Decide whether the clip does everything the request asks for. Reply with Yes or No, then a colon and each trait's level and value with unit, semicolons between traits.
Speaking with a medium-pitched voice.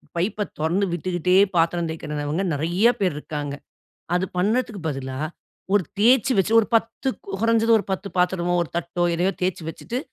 Yes: medium, 180 Hz